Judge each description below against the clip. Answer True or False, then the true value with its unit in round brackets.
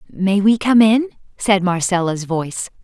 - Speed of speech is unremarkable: True (150 wpm)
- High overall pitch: True (200 Hz)